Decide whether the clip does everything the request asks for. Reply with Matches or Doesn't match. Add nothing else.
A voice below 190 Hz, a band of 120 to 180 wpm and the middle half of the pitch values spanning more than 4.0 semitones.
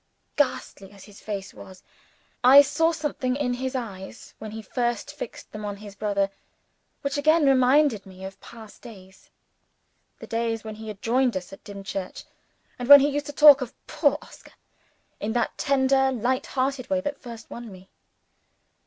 Doesn't match